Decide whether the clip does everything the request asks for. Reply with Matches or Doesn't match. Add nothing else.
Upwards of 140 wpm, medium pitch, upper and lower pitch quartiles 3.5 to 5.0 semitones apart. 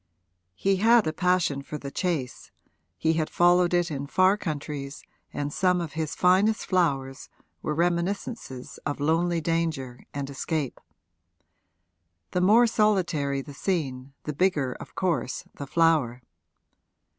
Doesn't match